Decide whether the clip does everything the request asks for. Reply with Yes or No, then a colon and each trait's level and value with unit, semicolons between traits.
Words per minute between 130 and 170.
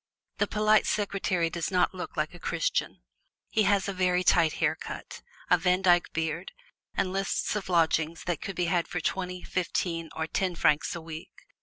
No: average, 180 wpm